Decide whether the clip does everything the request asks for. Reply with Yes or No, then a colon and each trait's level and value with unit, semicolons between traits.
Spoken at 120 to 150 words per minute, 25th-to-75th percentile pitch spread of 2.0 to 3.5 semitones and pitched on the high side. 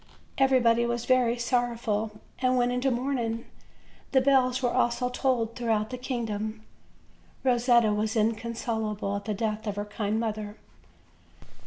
Yes: average, 140 wpm; narrow, 2.5 semitones; high, 235 Hz